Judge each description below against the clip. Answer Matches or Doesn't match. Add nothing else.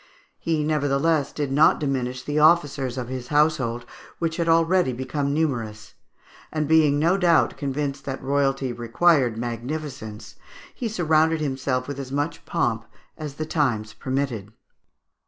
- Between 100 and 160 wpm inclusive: Matches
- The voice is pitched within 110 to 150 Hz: Matches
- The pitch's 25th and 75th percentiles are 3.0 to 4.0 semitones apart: Matches